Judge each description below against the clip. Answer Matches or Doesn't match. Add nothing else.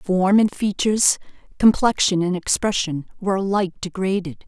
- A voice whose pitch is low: Doesn't match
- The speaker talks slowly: Matches